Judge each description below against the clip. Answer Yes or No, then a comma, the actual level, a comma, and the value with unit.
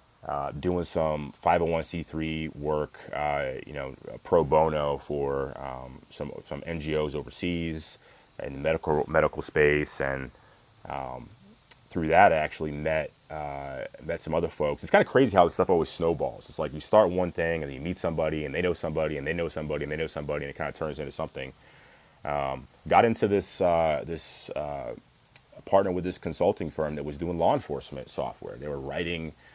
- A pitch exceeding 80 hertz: No, very low, 75 Hz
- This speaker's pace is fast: No, average, 185 wpm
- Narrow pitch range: Yes, narrow, 2.3 semitones